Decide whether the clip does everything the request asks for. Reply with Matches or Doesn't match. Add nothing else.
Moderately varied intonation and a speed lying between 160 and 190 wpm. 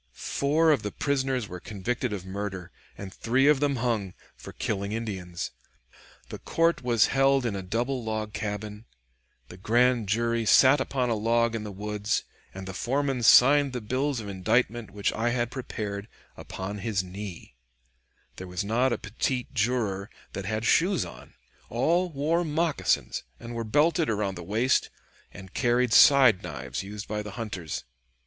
Matches